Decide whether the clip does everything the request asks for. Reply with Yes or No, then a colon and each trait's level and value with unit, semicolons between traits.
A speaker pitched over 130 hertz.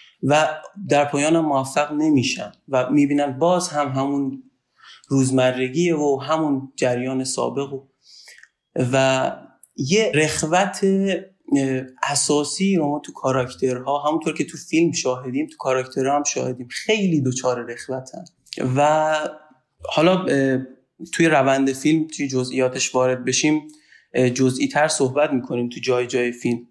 Yes: medium, 140 Hz